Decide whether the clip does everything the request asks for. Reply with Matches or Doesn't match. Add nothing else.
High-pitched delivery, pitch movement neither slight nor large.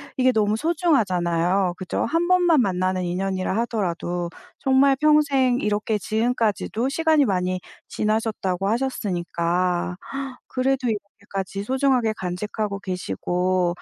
Doesn't match